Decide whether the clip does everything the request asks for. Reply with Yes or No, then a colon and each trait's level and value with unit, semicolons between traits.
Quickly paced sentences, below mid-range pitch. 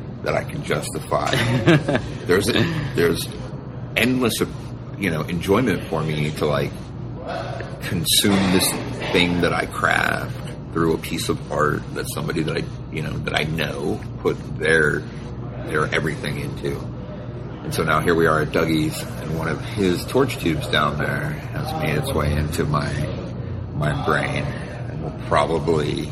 No: average, 150 wpm; very low, 90 Hz